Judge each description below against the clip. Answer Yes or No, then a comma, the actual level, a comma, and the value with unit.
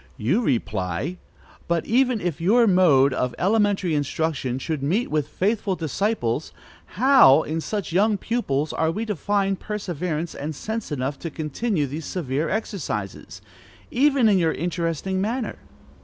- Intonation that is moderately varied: No, wide, 6.2 semitones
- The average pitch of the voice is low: No, medium, 175 Hz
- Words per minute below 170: Yes, average, 140 wpm